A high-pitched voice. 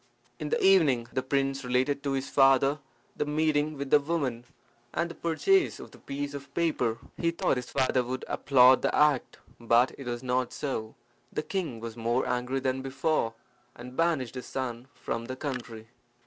No: low, 135 Hz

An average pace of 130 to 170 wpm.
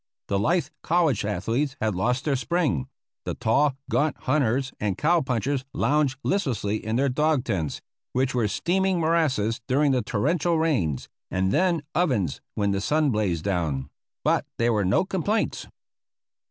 Yes: average, 155 wpm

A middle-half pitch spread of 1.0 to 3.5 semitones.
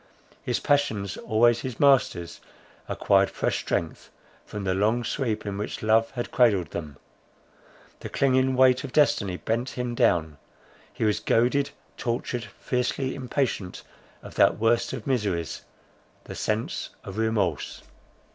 No: average, 4.3 semitones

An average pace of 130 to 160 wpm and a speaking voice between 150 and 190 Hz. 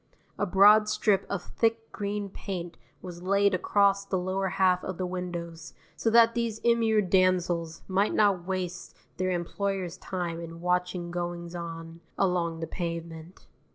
Yes: average, 150 wpm; medium, 185 Hz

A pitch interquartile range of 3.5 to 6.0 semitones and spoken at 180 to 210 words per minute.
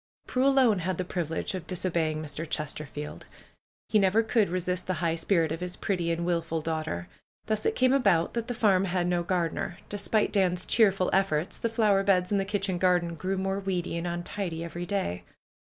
No: average, 3.0 semitones; average, 190 wpm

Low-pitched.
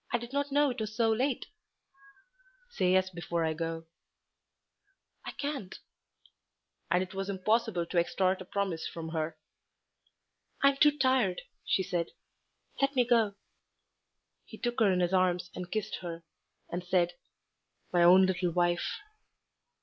No: medium, 185 Hz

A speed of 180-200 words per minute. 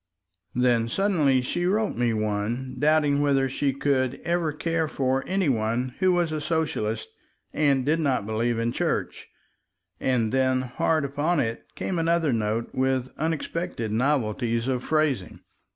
No: average, 145 wpm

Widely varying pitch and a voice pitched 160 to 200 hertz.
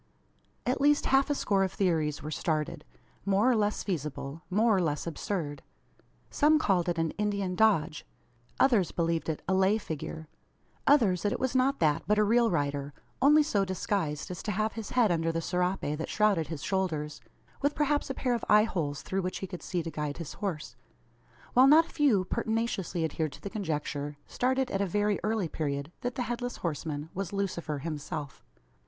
Yes: wide, 5.7 semitones; high, 190 Hz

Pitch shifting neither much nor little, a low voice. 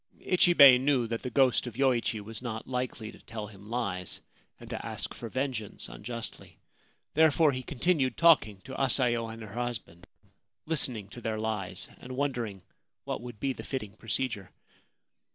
Yes: average, 3.4 semitones; low, 120 Hz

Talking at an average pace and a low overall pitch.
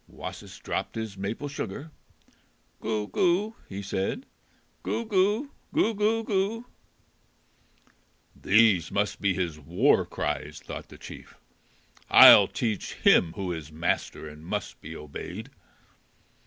No: slow, 120 wpm; low, 105 Hz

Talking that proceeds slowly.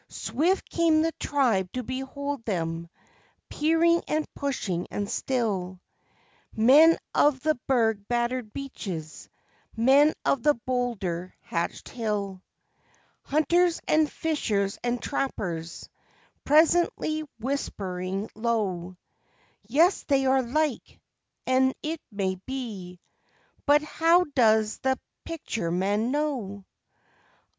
Yes: slow, 100 wpm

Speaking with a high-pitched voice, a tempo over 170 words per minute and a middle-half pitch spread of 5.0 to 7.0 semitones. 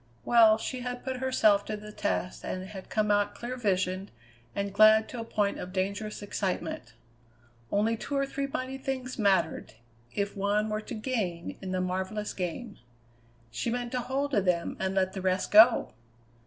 No: high, 210 Hz; average, 180 wpm; average, 4.1 semitones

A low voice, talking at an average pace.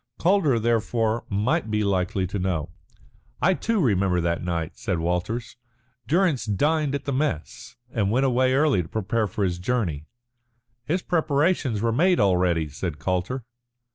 Yes: low, 110 Hz; average, 150 wpm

